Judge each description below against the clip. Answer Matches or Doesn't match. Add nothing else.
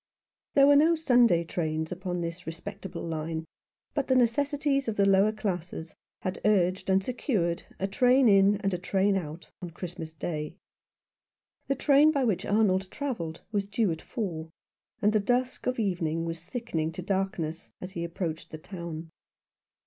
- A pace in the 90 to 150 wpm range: Doesn't match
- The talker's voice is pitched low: Doesn't match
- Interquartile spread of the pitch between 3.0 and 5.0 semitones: Doesn't match